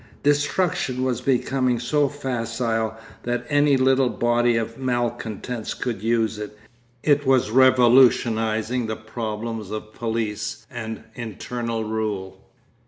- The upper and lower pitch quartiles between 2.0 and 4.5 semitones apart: Yes, narrow, 2.6 semitones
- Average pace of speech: No, slow, 110 wpm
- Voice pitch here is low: Yes, low, 120 Hz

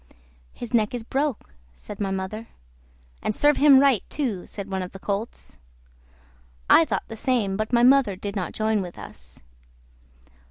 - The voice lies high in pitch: Yes, high, 215 Hz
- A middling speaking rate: Yes, average, 165 wpm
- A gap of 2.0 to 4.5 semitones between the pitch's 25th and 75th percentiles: Yes, average, 4.2 semitones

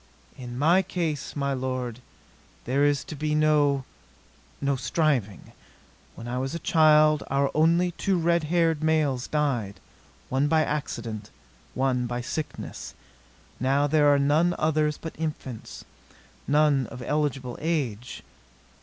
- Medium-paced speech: No, slow, 130 wpm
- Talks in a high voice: No, medium, 145 Hz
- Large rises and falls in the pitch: No, average, 3.2 semitones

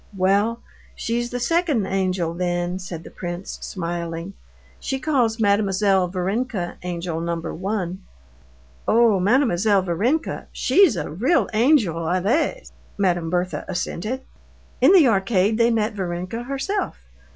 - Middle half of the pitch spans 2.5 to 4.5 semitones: No, average, 5.0 semitones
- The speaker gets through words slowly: Yes, slow, 120 wpm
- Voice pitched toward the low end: No, high, 195 Hz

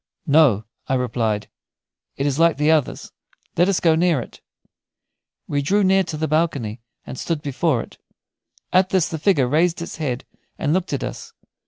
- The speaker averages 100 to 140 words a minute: No, average, 175 wpm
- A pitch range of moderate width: Yes, average, 4.1 semitones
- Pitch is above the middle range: No, medium, 155 Hz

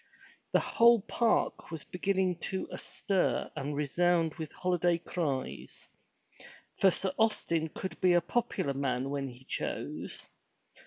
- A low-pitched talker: No, medium, 175 Hz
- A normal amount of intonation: Yes, average, 4.6 semitones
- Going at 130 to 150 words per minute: Yes, average, 140 wpm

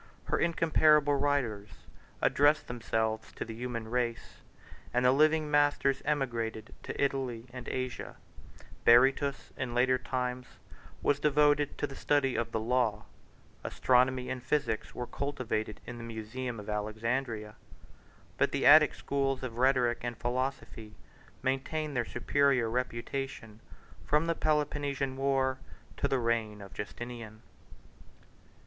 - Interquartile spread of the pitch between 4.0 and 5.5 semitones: No, average, 3.2 semitones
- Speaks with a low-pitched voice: Yes, low, 125 Hz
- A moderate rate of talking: No, slow, 125 wpm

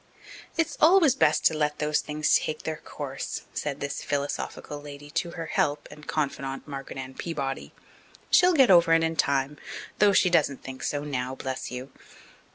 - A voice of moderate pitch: Yes, medium, 150 Hz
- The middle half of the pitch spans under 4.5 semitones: Yes, average, 3.0 semitones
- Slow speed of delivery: No, average, 170 wpm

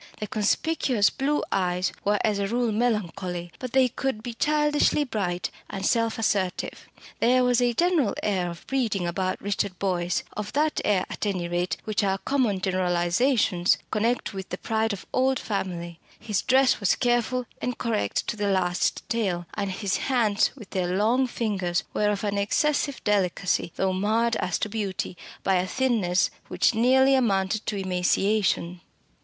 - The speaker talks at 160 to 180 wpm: Yes, average, 165 wpm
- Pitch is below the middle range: No, high, 205 Hz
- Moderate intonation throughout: Yes, average, 4.5 semitones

